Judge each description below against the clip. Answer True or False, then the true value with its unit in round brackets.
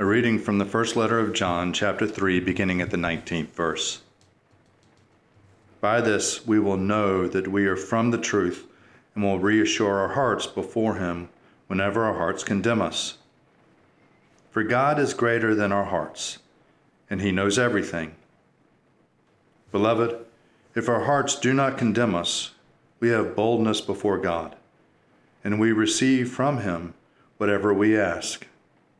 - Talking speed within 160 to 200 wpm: False (145 wpm)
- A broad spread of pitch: False (3.1 semitones)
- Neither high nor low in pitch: False (105 Hz)